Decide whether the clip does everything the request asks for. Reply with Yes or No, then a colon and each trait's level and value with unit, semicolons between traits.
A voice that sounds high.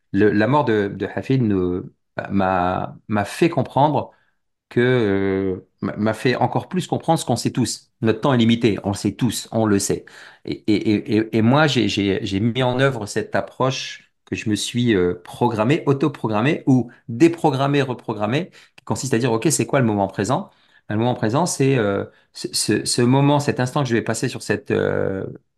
No: low, 115 Hz